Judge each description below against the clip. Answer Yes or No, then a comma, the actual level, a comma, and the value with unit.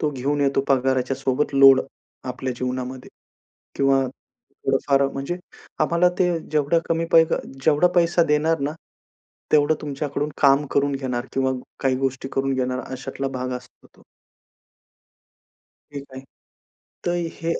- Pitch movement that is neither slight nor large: No, narrow, 2.1 semitones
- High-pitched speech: No, low, 135 Hz